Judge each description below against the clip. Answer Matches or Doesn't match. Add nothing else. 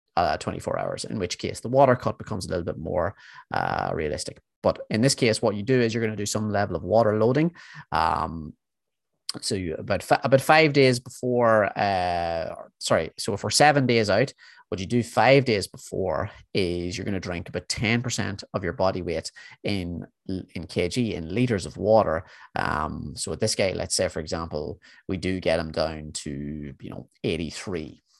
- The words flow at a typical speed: Matches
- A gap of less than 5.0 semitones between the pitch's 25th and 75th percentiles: Doesn't match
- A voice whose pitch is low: Matches